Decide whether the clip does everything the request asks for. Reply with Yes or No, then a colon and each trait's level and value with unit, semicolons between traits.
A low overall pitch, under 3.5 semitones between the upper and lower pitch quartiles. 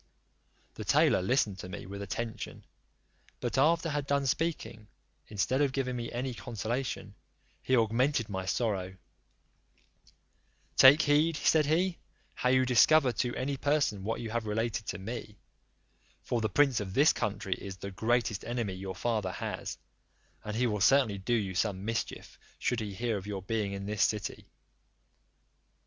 No: low, 115 Hz; average, 4.7 semitones